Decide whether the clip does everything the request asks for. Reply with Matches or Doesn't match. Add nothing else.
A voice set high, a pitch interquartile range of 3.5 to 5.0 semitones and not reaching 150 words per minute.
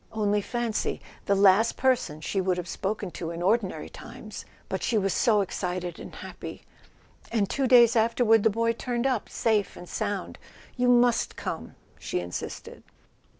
Doesn't match